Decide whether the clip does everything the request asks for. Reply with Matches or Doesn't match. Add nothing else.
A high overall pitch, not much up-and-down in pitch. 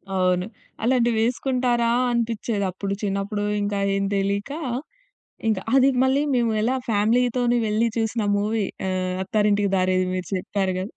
Doesn't match